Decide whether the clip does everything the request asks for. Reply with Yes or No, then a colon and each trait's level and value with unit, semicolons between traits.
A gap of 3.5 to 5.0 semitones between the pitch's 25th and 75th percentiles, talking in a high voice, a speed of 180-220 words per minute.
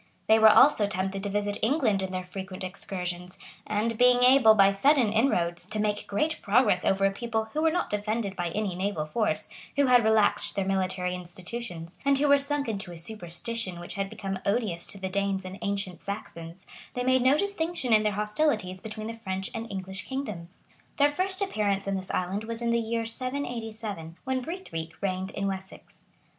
Yes: average, 3.9 semitones; high, 205 Hz; average, 190 wpm